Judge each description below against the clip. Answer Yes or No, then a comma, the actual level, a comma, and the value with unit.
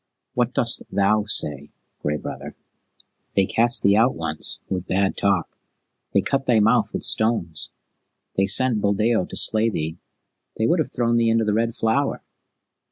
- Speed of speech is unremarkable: Yes, average, 165 wpm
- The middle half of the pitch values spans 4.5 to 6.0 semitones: No, average, 3.2 semitones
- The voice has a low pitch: Yes, low, 110 Hz